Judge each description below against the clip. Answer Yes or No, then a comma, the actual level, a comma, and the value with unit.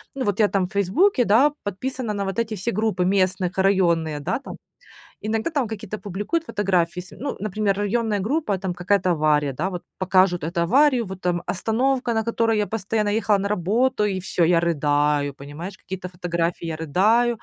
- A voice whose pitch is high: Yes, high, 195 Hz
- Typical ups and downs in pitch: Yes, average, 3.9 semitones